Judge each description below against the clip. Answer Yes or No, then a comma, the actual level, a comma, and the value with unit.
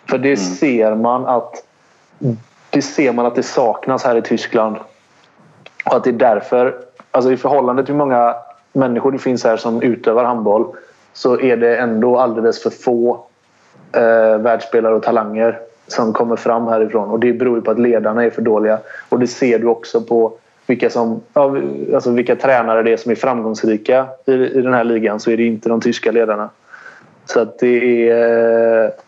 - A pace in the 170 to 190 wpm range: Yes, average, 185 wpm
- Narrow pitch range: Yes, narrow, 1.7 semitones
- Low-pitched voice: Yes, low, 115 Hz